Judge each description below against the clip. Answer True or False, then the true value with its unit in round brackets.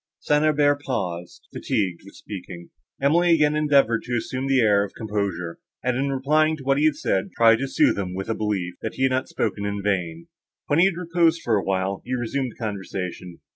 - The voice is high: False (115 Hz)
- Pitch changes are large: True (6.7 semitones)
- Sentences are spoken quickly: True (210 wpm)